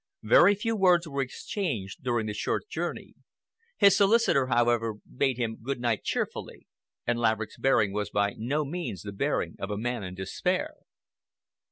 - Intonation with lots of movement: Yes, wide, 6.1 semitones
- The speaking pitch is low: Yes, low, 120 Hz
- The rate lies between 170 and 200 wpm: No, average, 160 wpm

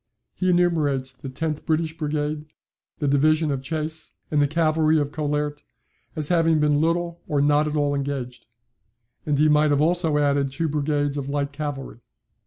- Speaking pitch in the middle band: Yes, medium, 150 Hz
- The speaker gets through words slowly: No, average, 170 wpm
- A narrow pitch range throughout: Yes, narrow, 1.7 semitones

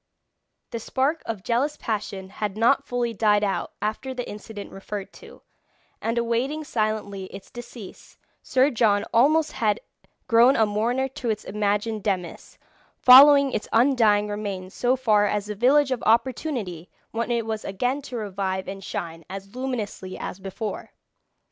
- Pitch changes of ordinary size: Yes, average, 3.7 semitones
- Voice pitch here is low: No, high, 220 Hz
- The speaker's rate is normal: Yes, average, 150 wpm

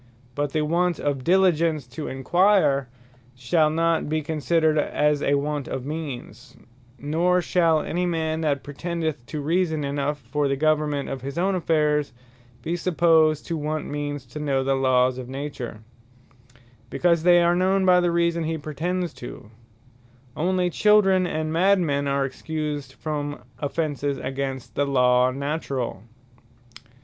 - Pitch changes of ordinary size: Yes, average, 3.3 semitones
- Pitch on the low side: No, medium, 150 Hz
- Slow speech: No, average, 145 wpm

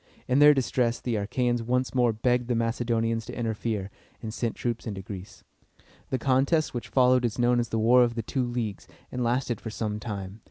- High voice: No, low, 120 Hz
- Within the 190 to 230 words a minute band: Yes, average, 200 wpm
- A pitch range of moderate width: No, narrow, 2.0 semitones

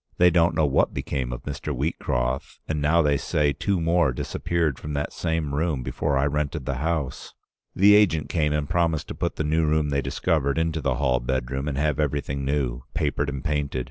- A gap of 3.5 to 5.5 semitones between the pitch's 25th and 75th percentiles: No, average, 2.8 semitones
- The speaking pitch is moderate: No, very low, 75 Hz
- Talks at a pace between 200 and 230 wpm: Yes, fast, 205 wpm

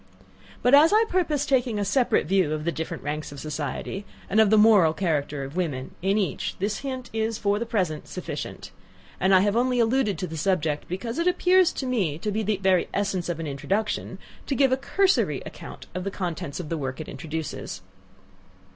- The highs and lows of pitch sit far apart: Yes, wide, 6.9 semitones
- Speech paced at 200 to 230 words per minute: Yes, fast, 205 wpm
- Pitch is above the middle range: Yes, high, 195 Hz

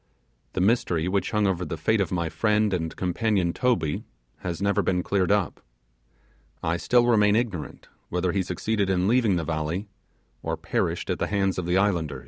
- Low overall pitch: Yes, very low, 95 Hz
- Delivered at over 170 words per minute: Yes, average, 180 wpm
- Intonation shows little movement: No, average, 3.3 semitones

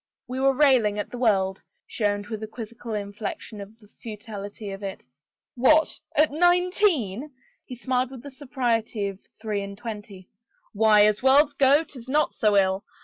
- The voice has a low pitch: No, high, 225 Hz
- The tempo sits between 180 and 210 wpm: Yes, average, 190 wpm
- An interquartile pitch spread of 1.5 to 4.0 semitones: No, average, 4.6 semitones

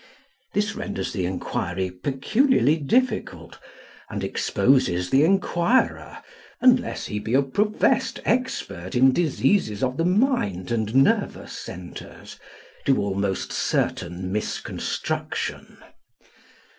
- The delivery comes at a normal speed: No, slow, 100 wpm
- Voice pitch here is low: Yes, low, 130 Hz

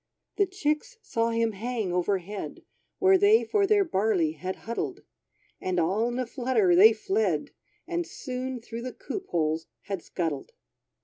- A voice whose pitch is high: Yes, high, 230 Hz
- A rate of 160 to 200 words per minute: No, average, 150 wpm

